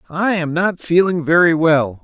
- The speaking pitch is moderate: Yes, medium, 165 Hz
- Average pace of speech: Yes, average, 175 wpm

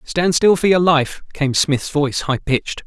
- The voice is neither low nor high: Yes, medium, 155 Hz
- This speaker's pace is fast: Yes, fast, 210 wpm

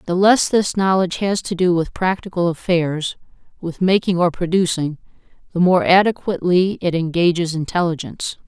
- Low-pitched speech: No, medium, 175 Hz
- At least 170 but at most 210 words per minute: No, average, 140 wpm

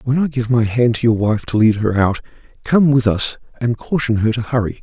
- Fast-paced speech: Yes, fast, 235 wpm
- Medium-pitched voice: No, low, 115 Hz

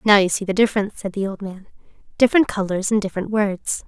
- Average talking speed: No, fast, 215 wpm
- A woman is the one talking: Yes, female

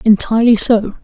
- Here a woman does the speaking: Yes, female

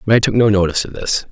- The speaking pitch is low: Yes, low, 100 Hz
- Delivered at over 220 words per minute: Yes, fast, 320 wpm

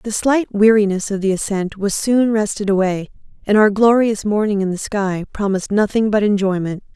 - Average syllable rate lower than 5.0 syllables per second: No, 5.2 syllables/s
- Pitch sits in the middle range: No, high, 205 Hz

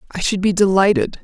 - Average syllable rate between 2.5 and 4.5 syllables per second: No, 6.0 syllables/s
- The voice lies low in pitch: No, high, 195 Hz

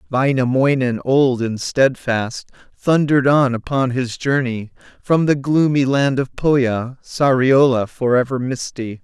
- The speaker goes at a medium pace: No, slow, 125 wpm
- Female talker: No, male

